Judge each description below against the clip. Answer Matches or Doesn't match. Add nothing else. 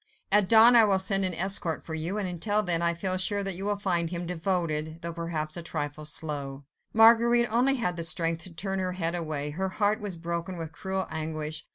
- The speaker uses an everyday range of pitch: Matches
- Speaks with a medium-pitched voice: Matches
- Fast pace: Matches